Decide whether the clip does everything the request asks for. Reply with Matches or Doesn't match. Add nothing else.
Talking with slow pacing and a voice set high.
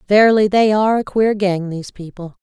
Doesn't match